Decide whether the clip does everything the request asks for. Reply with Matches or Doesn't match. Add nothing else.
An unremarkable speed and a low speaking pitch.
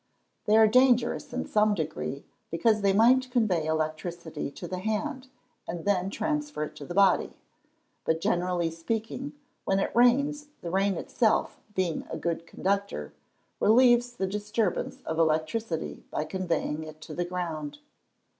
Doesn't match